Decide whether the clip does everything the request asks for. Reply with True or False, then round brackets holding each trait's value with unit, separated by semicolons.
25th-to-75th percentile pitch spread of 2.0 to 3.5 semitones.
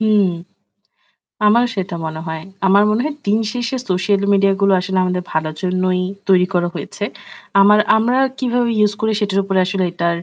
True (2.7 semitones)